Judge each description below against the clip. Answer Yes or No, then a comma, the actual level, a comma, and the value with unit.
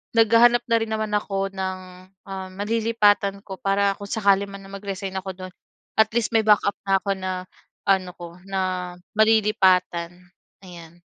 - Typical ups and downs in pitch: No, narrow, 2.1 semitones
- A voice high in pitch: Yes, high, 195 Hz